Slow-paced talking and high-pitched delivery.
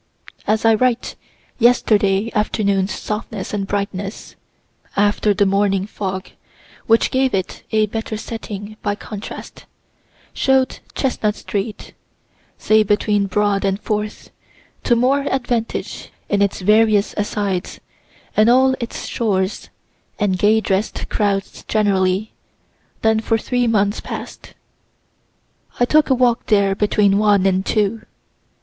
Yes: slow, 120 wpm; high, 210 Hz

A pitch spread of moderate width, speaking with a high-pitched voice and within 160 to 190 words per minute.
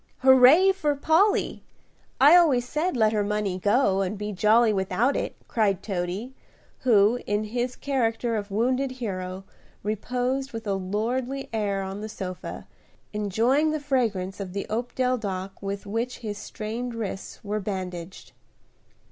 No: average, 4.2 semitones; high, 220 Hz; average, 140 wpm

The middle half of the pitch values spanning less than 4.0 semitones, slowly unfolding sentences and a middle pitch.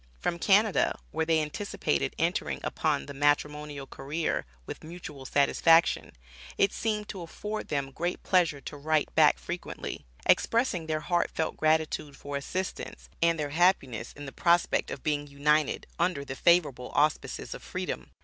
No: average, 3.3 semitones; average, 150 wpm; medium, 155 Hz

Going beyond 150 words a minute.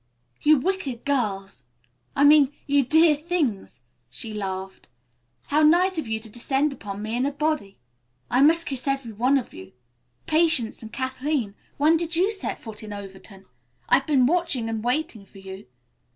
Yes: average, 165 wpm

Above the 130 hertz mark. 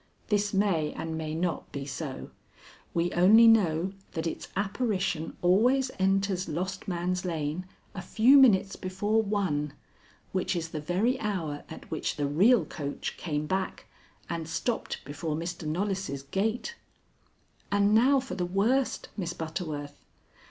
Yes: medium, 185 Hz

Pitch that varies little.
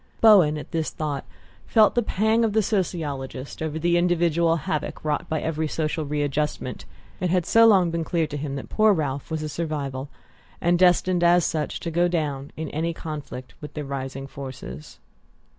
No: average, 3.2 semitones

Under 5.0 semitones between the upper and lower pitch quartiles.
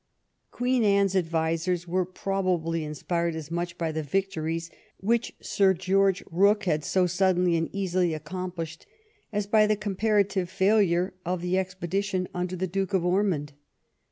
Yes: narrow, 2.6 semitones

